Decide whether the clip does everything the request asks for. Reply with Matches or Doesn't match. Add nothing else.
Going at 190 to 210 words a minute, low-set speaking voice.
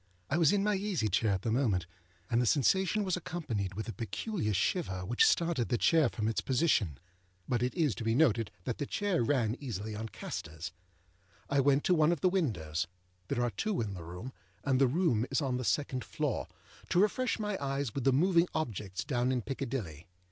Matches